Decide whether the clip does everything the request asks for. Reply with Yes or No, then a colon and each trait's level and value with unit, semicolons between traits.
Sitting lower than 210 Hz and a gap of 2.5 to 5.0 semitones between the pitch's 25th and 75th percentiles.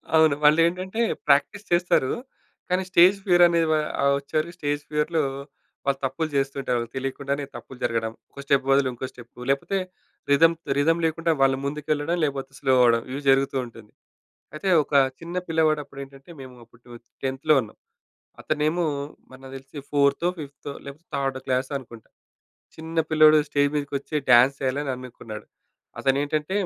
Yes: medium, 140 Hz; average, 2.9 semitones